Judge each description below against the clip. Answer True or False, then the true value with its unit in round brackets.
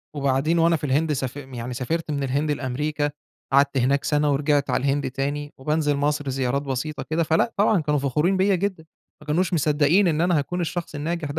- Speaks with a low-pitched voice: False (145 Hz)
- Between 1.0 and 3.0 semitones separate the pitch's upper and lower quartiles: True (2.7 semitones)